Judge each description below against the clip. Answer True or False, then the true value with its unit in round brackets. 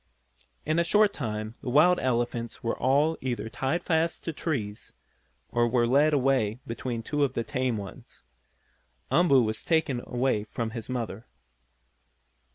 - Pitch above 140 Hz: False (130 Hz)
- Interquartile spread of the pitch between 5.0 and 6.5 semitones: False (4.4 semitones)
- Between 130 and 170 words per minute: True (150 wpm)